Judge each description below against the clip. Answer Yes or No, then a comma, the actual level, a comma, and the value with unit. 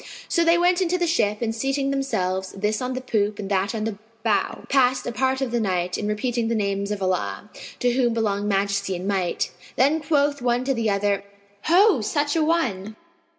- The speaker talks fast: Yes, fast, 210 wpm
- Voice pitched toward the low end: No, high, 225 Hz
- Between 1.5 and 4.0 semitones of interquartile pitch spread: No, average, 5.3 semitones